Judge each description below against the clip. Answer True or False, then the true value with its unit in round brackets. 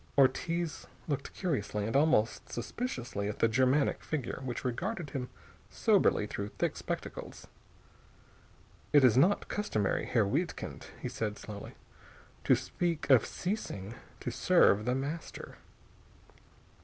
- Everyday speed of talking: False (120 wpm)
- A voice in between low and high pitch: False (130 Hz)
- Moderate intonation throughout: False (6.8 semitones)